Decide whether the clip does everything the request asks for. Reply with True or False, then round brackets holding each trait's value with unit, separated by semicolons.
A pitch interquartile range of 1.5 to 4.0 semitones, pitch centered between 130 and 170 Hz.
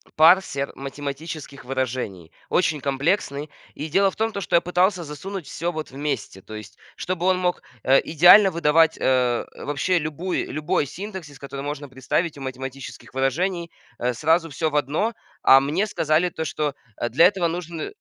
False (4.5 semitones; 155 Hz)